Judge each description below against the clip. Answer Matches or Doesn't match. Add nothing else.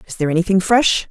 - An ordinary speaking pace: Doesn't match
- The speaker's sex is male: Doesn't match